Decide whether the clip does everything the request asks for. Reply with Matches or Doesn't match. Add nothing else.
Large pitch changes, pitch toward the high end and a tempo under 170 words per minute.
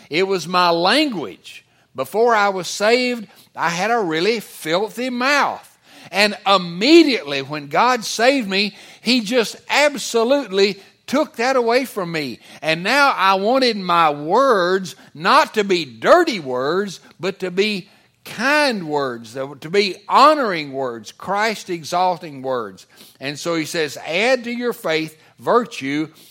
Matches